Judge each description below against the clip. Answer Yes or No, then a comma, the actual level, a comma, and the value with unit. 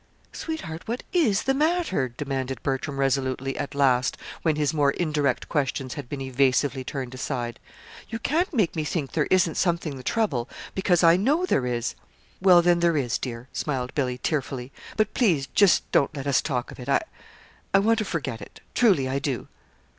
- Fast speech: No, average, 185 wpm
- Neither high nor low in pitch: Yes, medium, 145 Hz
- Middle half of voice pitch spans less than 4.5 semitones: No, wide, 5.5 semitones